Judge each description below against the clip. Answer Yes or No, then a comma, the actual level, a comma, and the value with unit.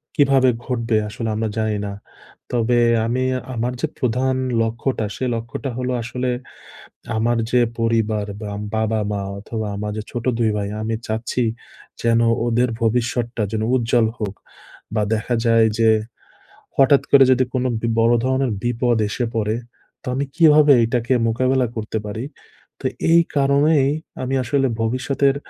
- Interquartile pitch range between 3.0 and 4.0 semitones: No, narrow, 2.5 semitones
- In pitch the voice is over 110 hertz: Yes, low, 120 Hz